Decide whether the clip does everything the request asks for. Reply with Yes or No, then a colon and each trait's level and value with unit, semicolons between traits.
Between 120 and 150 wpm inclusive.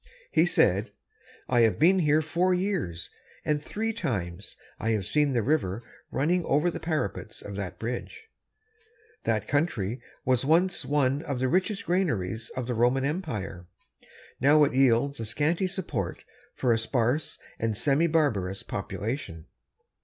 Yes: average, 145 wpm